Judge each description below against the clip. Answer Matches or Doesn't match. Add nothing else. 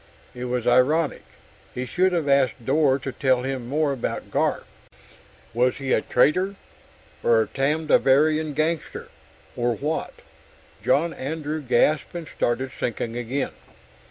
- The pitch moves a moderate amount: Matches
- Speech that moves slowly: Matches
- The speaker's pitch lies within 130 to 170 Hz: Matches